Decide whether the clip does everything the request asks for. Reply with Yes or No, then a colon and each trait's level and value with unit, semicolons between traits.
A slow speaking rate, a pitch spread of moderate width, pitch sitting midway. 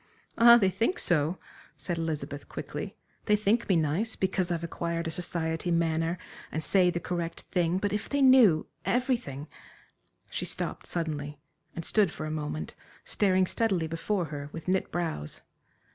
No: average, 160 wpm; average, 3.6 semitones; medium, 170 Hz